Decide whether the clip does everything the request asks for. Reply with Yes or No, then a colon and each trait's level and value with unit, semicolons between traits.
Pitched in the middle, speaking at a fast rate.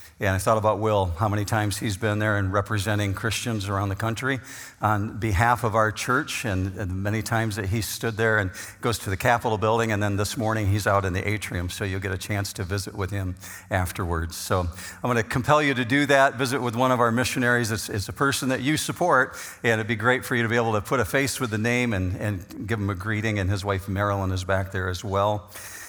No: low, 110 Hz; fast, 255 wpm